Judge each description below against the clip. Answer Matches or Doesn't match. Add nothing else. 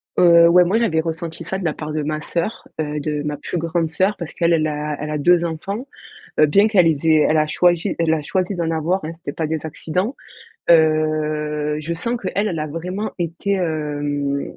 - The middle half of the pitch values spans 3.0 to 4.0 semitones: Doesn't match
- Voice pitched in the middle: Matches